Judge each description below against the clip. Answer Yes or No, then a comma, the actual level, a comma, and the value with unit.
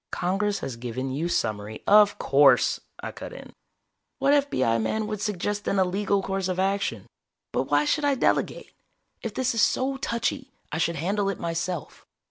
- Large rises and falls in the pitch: Yes, wide, 6.5 semitones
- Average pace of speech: Yes, average, 175 wpm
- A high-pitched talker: Yes, high, 195 Hz